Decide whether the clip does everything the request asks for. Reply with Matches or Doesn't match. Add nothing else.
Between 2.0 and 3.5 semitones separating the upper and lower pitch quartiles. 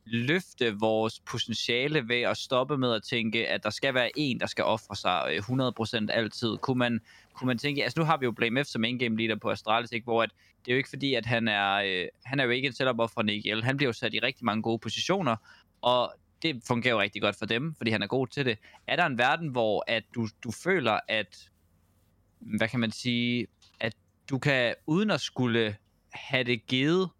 Matches